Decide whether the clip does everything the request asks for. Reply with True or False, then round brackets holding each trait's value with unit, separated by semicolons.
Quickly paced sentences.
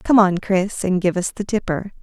True (235 wpm)